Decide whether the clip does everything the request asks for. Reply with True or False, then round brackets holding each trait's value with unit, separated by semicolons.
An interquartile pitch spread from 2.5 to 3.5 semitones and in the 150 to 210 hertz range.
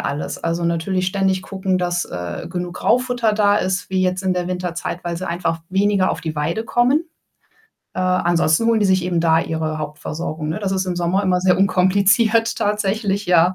True (2.9 semitones; 185 Hz)